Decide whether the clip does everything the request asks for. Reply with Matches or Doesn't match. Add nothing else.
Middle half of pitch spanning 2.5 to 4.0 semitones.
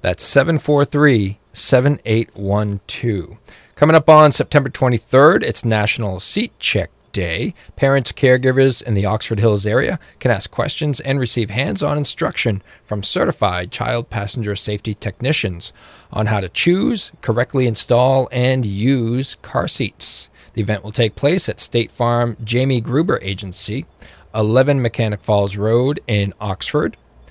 Doesn't match